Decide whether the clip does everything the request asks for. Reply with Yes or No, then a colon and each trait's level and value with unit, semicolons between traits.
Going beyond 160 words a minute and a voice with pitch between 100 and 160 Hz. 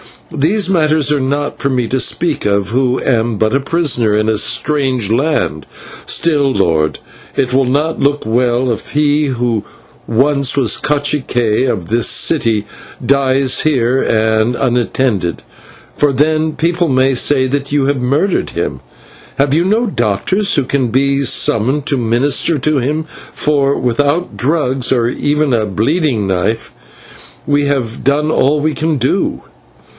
No: average, 150 wpm; low, 135 Hz